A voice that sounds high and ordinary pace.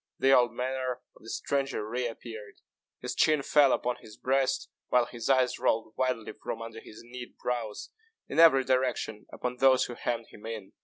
No: low, 125 Hz; average, 185 wpm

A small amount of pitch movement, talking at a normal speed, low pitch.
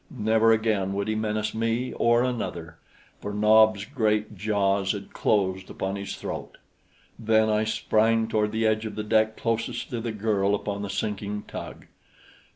Yes: narrow, 1.6 semitones; average, 160 wpm; low, 110 Hz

